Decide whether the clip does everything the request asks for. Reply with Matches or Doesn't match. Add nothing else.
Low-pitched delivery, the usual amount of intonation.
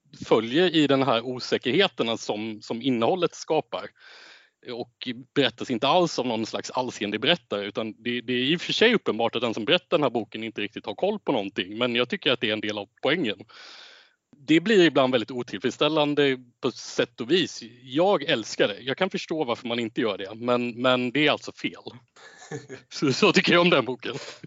Matches